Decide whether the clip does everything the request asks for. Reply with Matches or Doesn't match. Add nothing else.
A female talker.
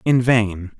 Doesn't match